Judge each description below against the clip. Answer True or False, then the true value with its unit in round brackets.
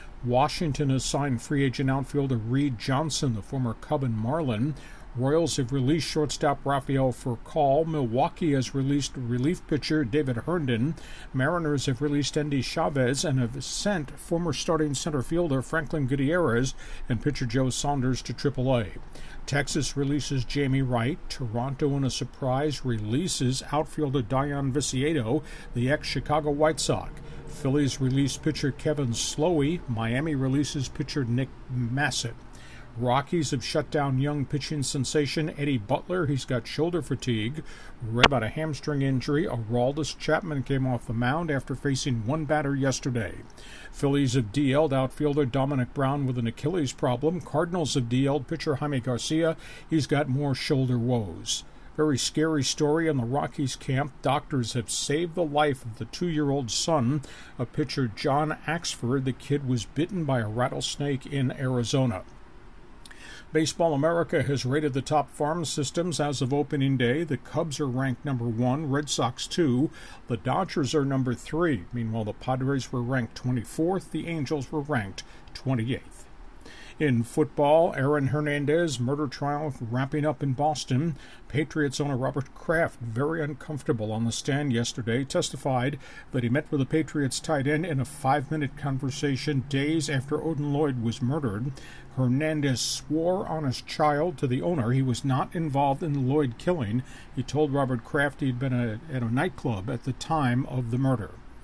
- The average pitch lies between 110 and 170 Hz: True (140 Hz)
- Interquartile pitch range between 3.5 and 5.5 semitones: False (3.1 semitones)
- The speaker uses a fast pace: False (155 wpm)